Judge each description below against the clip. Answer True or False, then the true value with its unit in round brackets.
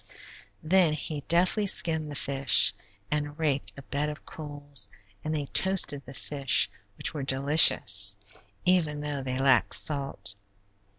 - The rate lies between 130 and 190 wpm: True (135 wpm)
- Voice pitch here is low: False (145 Hz)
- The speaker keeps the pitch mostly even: True (2.2 semitones)